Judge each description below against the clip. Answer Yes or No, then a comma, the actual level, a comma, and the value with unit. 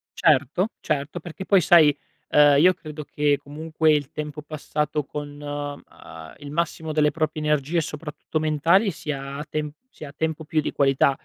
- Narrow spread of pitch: Yes, narrow, 1.5 semitones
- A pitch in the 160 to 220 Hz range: No, medium, 150 Hz